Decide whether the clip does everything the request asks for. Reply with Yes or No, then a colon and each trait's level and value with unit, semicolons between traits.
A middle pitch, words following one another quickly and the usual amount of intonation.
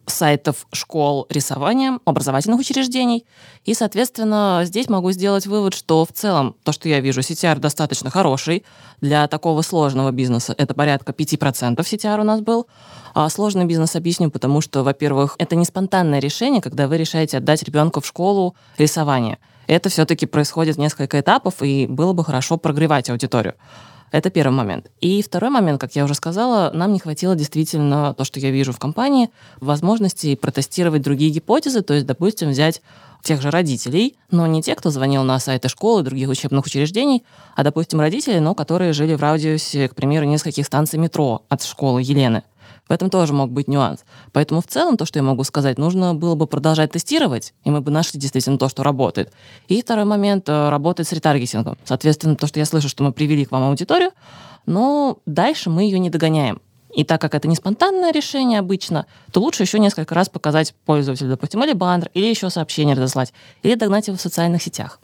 Yes: medium, 155 Hz; fast, 185 wpm; average, 4.7 semitones